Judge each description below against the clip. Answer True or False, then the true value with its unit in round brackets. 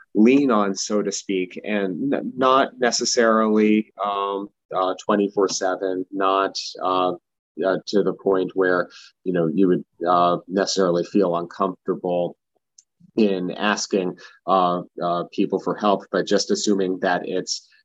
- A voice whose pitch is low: True (95 Hz)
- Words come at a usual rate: False (130 wpm)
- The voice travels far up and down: False (2.4 semitones)